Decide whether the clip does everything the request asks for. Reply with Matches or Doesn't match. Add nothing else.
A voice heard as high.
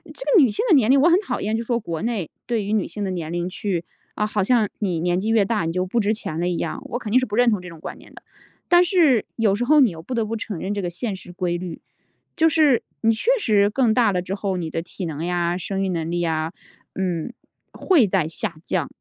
Matches